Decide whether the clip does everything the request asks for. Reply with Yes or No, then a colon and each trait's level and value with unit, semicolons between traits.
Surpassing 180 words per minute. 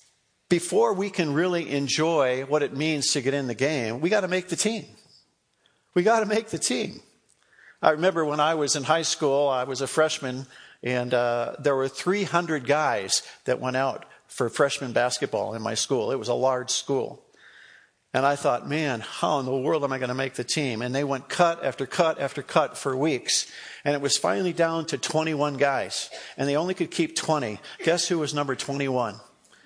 Yes: average, 200 wpm